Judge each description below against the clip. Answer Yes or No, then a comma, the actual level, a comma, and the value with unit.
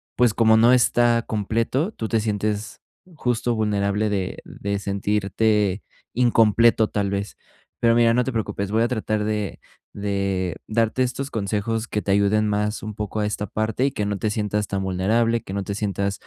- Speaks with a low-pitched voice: Yes, low, 105 Hz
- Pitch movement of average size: No, narrow, 2.2 semitones